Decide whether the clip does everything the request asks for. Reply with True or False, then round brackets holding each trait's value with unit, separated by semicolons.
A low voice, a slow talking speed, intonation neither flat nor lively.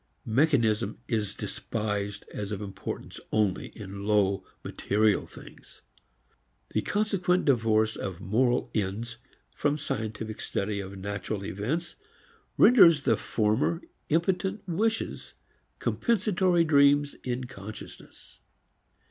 False (110 Hz; 100 wpm; 7.5 semitones)